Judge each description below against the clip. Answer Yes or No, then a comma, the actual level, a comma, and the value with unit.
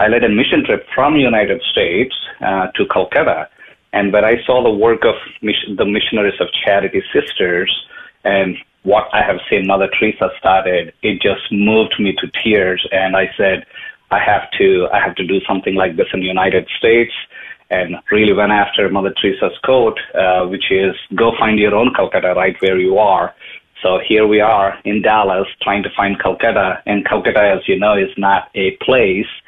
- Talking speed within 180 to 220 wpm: Yes, average, 190 wpm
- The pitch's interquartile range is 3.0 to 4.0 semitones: Yes, average, 3.4 semitones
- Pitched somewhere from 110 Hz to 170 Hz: No, low, 100 Hz